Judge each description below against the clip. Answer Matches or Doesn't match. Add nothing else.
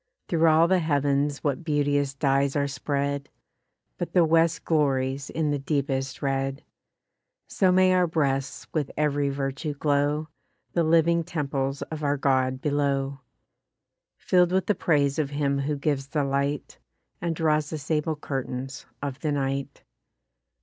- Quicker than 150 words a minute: Doesn't match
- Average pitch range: Doesn't match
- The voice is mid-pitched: Matches